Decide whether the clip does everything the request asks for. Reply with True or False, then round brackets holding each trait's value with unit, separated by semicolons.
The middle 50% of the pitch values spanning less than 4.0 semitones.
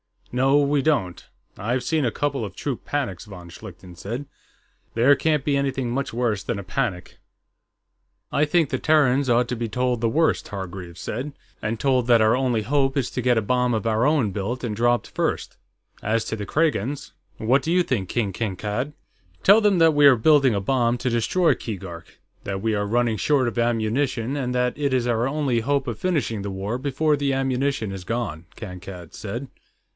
False (4.4 semitones)